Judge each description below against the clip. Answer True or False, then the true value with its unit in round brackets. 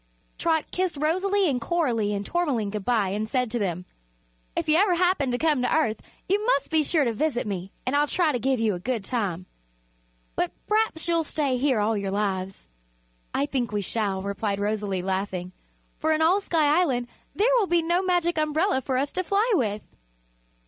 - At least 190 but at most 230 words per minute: True (195 wpm)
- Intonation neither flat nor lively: False (8.1 semitones)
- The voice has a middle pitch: False (260 Hz)